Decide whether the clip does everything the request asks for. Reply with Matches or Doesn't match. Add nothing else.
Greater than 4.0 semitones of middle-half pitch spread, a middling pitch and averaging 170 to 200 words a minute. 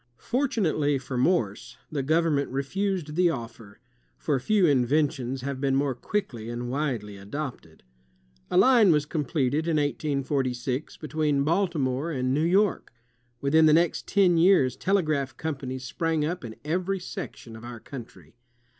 Doesn't match